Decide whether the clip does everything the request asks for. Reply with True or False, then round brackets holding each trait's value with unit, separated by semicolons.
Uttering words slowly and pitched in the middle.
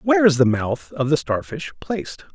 False (205 wpm; 155 Hz)